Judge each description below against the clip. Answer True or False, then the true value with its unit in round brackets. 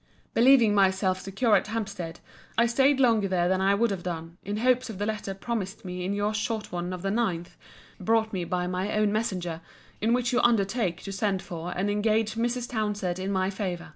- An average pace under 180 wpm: False (205 wpm)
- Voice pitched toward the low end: False (205 Hz)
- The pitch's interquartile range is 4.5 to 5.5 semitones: False (3.4 semitones)